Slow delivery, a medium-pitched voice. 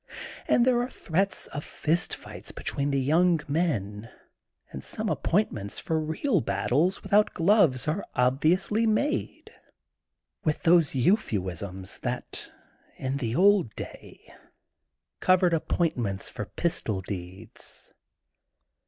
Yes: slow, 120 wpm; medium, 155 Hz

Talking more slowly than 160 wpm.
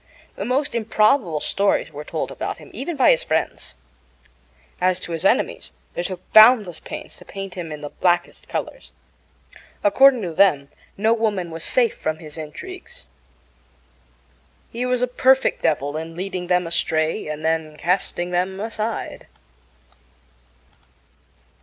Yes: average, 140 wpm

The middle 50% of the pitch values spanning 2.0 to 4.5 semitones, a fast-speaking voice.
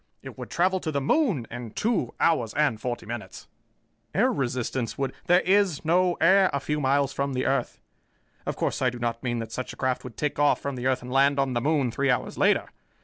Yes: average, 4.1 semitones; fast, 230 wpm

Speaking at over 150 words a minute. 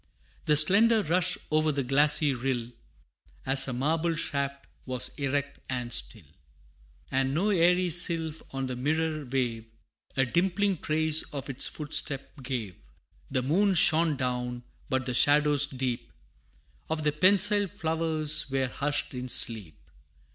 No: slow, 135 wpm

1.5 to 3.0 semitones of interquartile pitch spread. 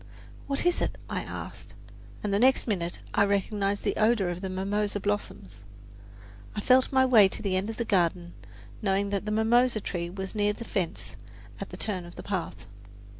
Yes: average, 2.7 semitones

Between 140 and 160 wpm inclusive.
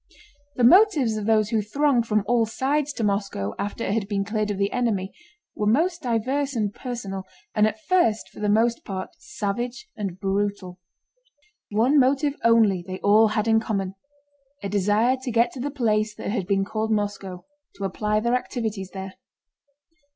No: average, 175 wpm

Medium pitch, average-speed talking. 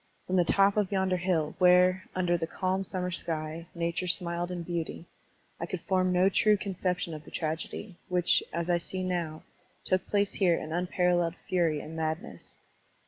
Yes: medium, 180 Hz; average, 180 wpm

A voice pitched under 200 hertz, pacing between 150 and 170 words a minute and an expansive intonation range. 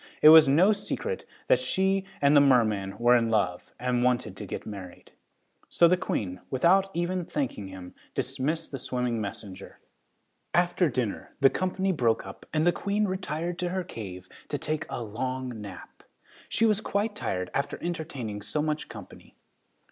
Yes: medium, 140 Hz; average, 165 wpm; wide, 8.0 semitones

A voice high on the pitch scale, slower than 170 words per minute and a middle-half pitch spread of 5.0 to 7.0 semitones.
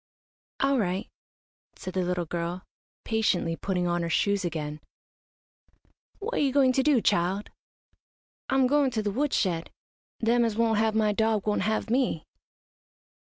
Yes: high, 210 Hz; average, 150 wpm; average, 5.3 semitones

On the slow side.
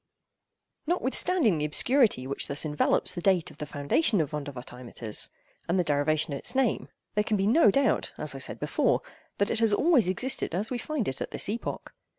No: average, 195 wpm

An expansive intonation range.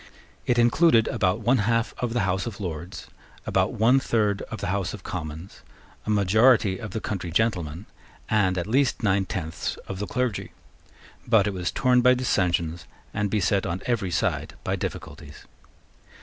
No: average, 4.2 semitones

